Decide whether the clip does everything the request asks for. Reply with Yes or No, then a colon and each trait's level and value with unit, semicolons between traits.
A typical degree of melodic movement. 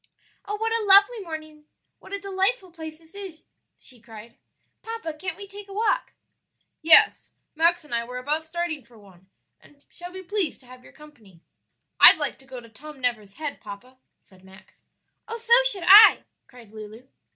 No: wide, 8.0 semitones